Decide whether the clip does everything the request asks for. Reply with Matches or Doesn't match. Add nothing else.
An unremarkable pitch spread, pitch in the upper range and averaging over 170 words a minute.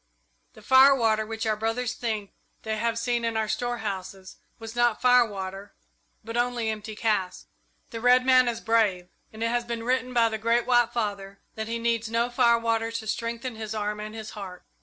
Doesn't match